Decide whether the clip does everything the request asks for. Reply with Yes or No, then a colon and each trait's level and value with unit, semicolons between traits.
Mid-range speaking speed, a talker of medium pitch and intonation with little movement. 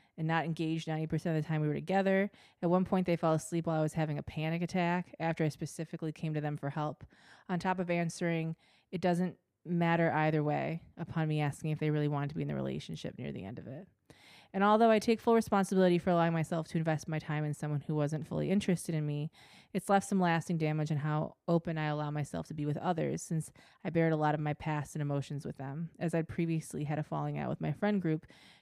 No: fast, 245 wpm; medium, 160 Hz; narrow, 2.3 semitones